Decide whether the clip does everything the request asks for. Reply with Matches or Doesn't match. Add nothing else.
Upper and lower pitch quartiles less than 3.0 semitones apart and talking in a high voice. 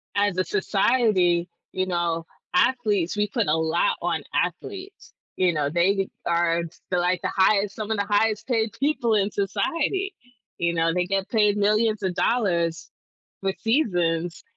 Doesn't match